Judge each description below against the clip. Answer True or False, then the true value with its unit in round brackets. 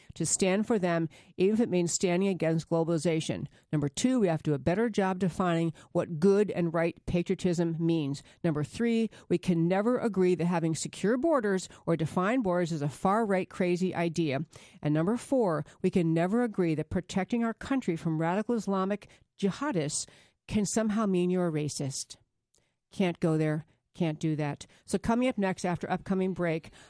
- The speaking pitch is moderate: True (175 Hz)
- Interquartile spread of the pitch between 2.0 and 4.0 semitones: True (3.3 semitones)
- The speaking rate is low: False (180 wpm)